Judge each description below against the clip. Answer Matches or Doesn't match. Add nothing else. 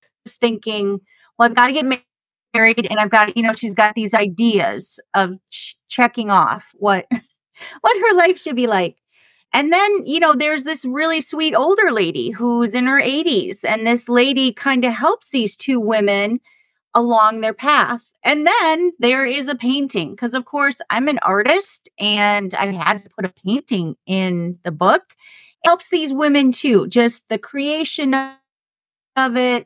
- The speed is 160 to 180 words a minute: Matches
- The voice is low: Doesn't match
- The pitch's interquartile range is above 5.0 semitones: Matches